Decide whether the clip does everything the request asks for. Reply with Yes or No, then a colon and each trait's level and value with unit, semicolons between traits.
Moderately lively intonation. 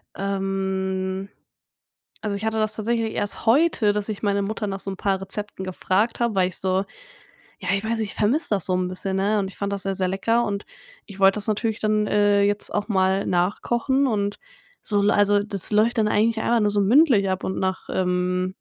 No: narrow, 2.1 semitones